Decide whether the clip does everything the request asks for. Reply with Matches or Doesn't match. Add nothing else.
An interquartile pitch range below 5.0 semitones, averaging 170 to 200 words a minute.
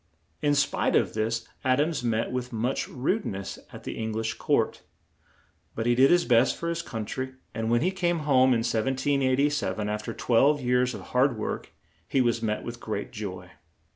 Matches